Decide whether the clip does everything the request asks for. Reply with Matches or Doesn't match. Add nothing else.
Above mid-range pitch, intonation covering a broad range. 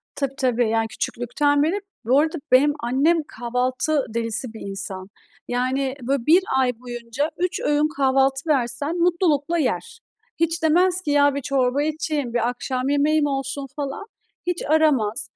Doesn't match